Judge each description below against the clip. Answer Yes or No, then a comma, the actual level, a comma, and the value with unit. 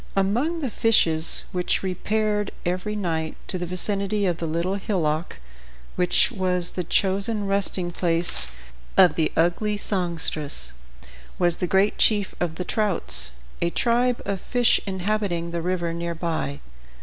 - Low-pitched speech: No, medium, 185 Hz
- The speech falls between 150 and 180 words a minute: No, average, 140 wpm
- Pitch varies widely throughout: No, average, 3.3 semitones